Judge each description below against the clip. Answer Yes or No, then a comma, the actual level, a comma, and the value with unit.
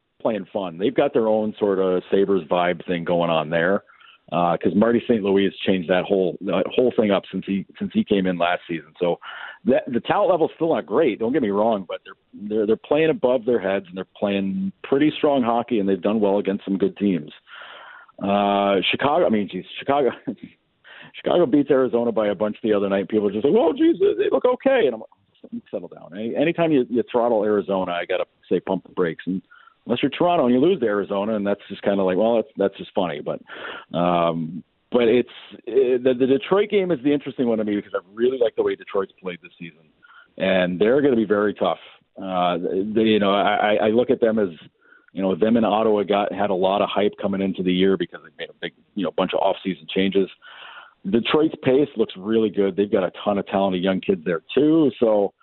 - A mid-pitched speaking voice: No, low, 105 Hz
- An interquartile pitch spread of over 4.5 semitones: Yes, wide, 5.4 semitones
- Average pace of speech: No, fast, 235 wpm